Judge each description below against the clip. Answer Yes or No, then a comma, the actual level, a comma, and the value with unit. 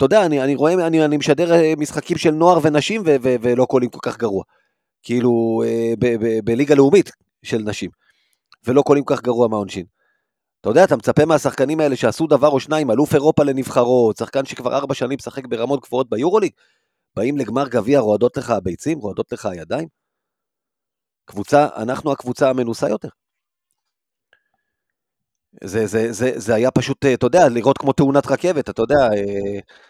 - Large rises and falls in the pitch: No, average, 4.0 semitones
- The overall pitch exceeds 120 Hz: Yes, low, 135 Hz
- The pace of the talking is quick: Yes, fast, 160 wpm